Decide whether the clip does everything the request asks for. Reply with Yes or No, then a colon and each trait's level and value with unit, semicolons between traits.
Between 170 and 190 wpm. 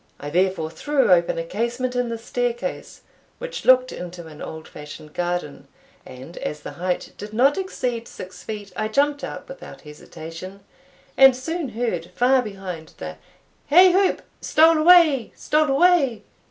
No: average, 155 wpm